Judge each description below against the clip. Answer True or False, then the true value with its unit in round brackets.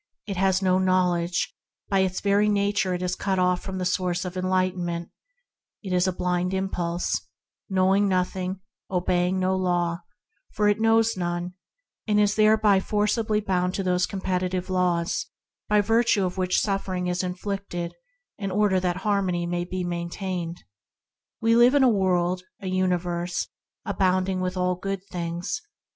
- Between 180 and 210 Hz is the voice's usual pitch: True (185 Hz)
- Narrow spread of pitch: True (1.7 semitones)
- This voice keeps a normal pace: True (155 wpm)